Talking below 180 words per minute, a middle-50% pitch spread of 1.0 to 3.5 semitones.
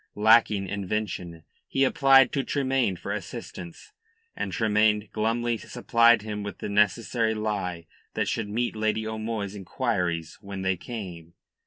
Yes: slow, 135 wpm; average, 3.2 semitones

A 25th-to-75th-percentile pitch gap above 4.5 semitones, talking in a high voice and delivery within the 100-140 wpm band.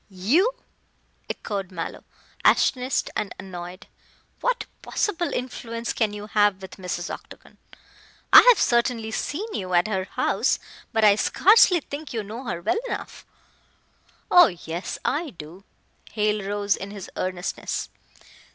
Yes: average, 5.1 semitones; high, 210 Hz; slow, 135 wpm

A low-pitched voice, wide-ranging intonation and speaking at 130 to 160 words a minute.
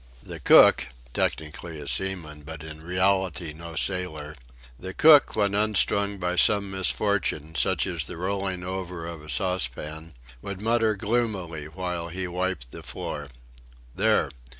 No: very low, 90 Hz; average, 3.8 semitones; average, 140 wpm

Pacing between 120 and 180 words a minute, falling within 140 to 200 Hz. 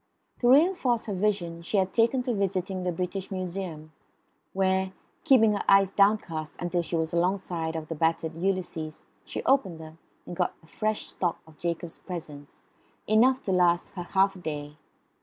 Yes: average, 170 wpm; medium, 185 Hz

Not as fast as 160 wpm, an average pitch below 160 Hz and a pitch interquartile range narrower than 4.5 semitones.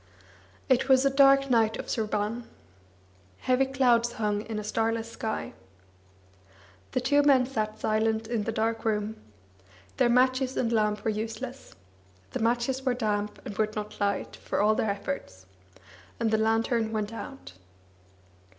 No: average, 150 wpm; high, 225 Hz; average, 2.9 semitones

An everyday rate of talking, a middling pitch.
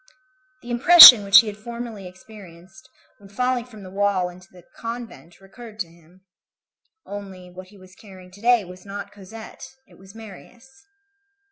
No: average, 160 wpm; high, 200 Hz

